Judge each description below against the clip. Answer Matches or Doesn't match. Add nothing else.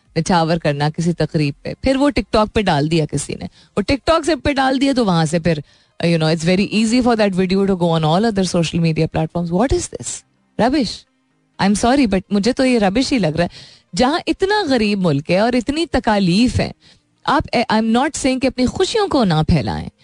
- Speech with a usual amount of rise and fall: Doesn't match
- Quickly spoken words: Matches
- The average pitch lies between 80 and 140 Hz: Doesn't match